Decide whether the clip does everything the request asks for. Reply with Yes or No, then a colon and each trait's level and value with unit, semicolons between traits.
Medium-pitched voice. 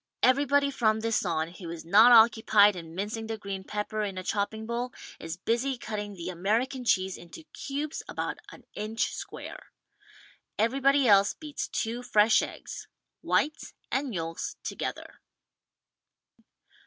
No: high, 220 Hz